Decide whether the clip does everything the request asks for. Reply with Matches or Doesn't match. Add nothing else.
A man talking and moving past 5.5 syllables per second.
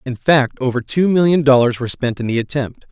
Matches